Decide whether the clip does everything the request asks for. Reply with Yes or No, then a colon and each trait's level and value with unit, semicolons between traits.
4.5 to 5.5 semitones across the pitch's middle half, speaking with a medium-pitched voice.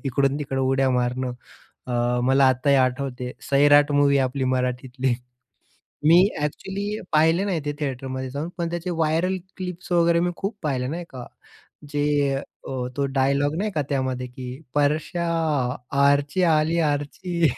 No: average, 3.9 semitones; medium, 145 Hz